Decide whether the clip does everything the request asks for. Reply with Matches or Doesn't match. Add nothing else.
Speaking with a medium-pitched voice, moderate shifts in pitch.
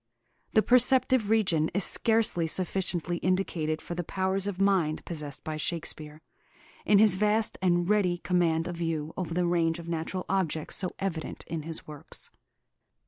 Matches